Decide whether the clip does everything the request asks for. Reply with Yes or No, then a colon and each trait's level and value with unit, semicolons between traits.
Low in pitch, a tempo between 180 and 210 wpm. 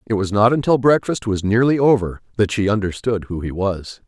Yes: low, 110 Hz; fast, 205 wpm